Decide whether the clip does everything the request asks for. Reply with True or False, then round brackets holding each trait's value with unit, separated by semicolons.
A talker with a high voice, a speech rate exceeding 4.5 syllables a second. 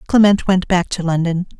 False (180 Hz; 5.2 syllables/s)